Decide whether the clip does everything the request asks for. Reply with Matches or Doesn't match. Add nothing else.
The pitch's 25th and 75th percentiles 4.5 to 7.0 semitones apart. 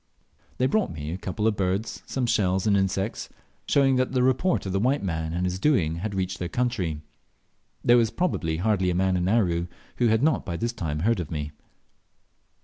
Matches